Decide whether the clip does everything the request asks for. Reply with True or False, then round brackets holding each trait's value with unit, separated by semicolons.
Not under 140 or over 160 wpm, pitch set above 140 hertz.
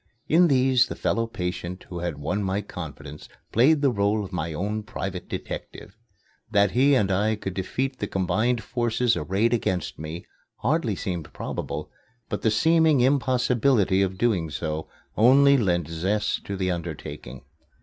False (155 wpm; 105 Hz)